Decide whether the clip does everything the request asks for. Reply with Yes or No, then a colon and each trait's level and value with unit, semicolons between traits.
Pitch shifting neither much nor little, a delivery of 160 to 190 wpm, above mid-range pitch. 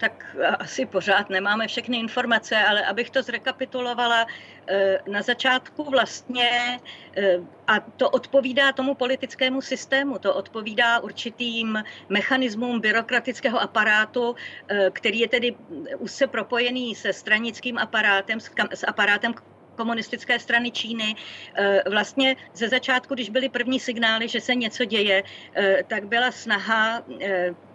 No: average, 3.1 semitones; average, 120 wpm; high, 235 Hz